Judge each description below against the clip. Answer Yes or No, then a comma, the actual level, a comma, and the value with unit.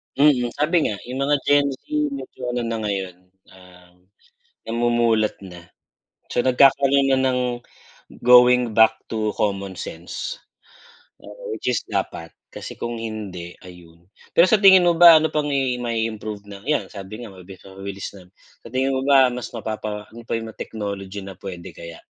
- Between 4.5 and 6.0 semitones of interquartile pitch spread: Yes, average, 5.2 semitones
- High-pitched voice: No, low, 115 Hz